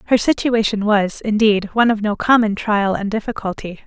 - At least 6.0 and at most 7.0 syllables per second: No, 5.4 syllables/s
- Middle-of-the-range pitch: No, high, 215 Hz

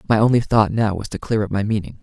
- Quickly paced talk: Yes, fast, 295 wpm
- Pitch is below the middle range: Yes, low, 105 Hz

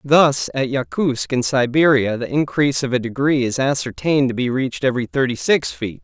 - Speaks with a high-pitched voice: No, low, 130 Hz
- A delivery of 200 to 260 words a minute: No, average, 190 wpm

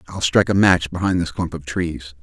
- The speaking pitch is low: Yes, very low, 85 Hz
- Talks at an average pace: No, fast, 245 wpm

